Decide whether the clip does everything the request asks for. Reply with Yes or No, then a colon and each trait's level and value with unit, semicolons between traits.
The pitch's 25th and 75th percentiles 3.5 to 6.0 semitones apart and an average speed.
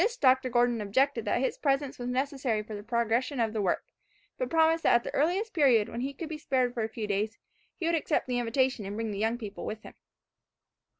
No: average, 4.1 semitones; fast, 240 wpm